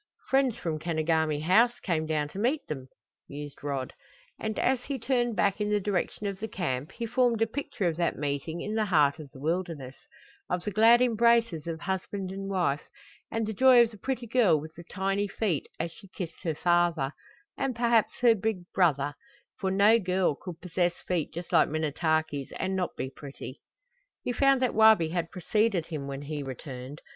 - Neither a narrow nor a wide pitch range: No, wide, 5.9 semitones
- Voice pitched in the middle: Yes, medium, 180 Hz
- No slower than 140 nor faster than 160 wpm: No, average, 190 wpm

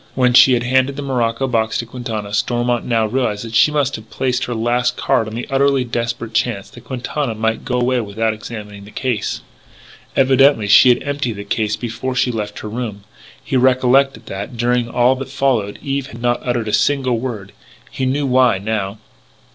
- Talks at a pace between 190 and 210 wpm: Yes, average, 195 wpm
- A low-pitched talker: Yes, low, 120 Hz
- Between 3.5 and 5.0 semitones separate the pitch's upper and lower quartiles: No, average, 2.9 semitones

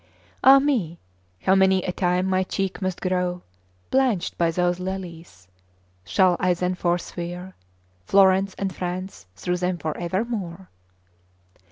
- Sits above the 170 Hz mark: Yes, medium, 185 Hz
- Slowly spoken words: Yes, slow, 130 wpm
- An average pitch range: No, narrow, 1.4 semitones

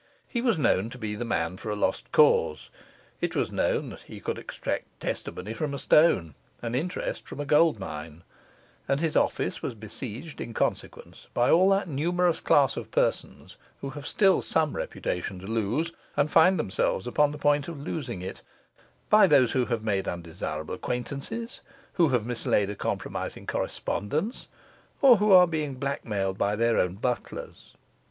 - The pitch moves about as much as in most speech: No, wide, 7.4 semitones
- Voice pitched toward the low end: Yes, low, 130 Hz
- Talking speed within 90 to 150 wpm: No, average, 165 wpm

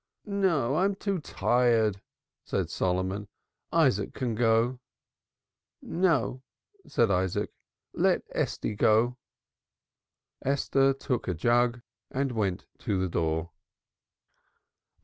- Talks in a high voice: No, low, 120 Hz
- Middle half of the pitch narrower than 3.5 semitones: No, wide, 5.4 semitones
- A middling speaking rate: No, slow, 95 wpm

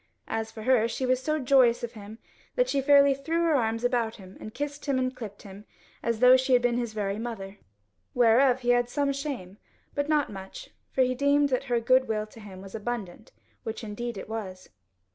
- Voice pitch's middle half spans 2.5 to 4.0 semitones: Yes, average, 3.7 semitones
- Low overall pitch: No, high, 240 Hz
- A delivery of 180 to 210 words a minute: Yes, fast, 205 wpm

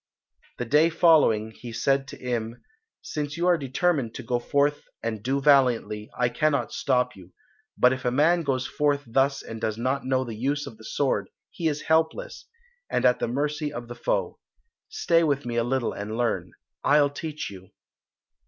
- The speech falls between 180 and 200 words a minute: Yes, average, 185 wpm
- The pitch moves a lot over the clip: No, average, 3.8 semitones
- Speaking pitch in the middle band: No, low, 130 Hz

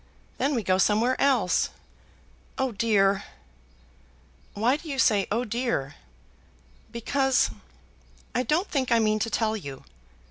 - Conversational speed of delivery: No, slow, 130 wpm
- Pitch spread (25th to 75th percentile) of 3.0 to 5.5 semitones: Yes, average, 4.0 semitones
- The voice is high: Yes, high, 230 Hz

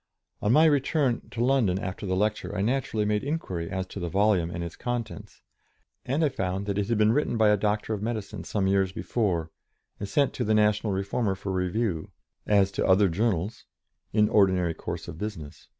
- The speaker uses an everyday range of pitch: Yes, average, 3.3 semitones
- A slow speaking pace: No, average, 200 wpm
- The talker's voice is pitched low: Yes, low, 105 Hz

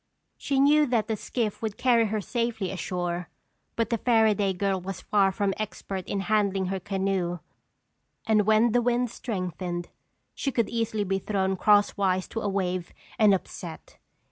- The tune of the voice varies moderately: Yes, average, 3.0 semitones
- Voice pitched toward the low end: No, high, 205 Hz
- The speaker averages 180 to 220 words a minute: No, average, 160 wpm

